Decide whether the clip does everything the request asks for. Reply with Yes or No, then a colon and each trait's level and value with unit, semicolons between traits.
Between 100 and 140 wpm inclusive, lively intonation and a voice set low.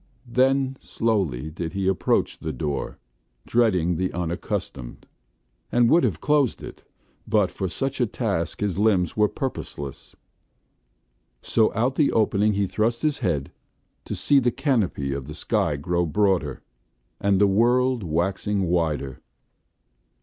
Yes: slow, 135 wpm; wide, 5.9 semitones; low, 100 Hz